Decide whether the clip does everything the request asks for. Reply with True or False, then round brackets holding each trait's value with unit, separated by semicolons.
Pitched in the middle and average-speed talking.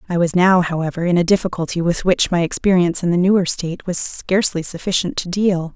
False (175 Hz; 210 wpm)